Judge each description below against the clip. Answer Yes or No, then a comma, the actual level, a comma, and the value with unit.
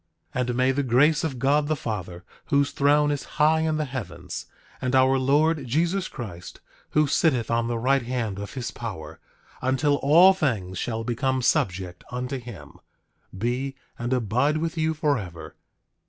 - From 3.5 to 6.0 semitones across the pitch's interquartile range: Yes, average, 4.1 semitones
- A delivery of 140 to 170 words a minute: Yes, average, 165 wpm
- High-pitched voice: No, low, 130 Hz